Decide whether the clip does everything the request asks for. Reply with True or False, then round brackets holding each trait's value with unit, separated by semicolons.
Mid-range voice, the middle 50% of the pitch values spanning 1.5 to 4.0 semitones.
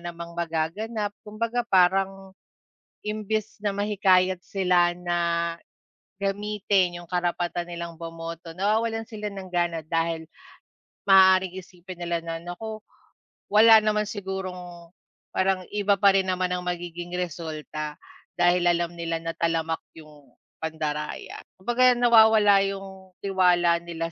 True (180 Hz; 2.8 semitones)